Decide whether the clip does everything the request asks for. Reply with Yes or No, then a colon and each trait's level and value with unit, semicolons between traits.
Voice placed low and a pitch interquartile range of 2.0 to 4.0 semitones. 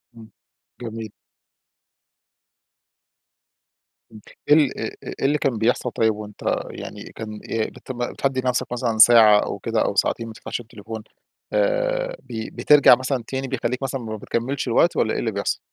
Yes: low, 120 Hz; average, 3.4 semitones